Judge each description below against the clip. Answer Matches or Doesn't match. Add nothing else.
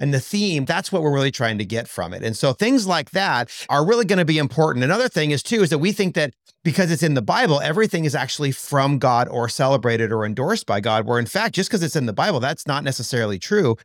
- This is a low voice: Doesn't match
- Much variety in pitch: Matches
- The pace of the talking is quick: Matches